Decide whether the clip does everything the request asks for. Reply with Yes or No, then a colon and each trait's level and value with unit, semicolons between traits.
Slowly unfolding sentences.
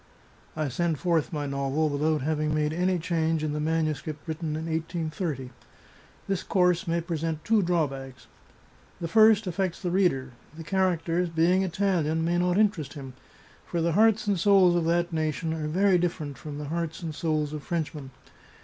No: average, 170 wpm